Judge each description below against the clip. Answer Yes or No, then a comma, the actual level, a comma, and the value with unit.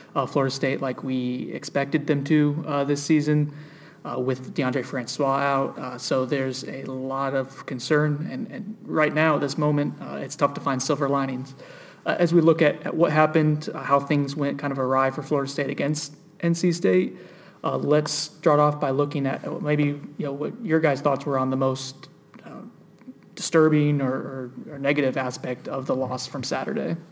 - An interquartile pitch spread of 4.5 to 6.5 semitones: No, narrow, 2.5 semitones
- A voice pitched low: No, medium, 145 Hz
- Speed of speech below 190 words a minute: No, average, 195 wpm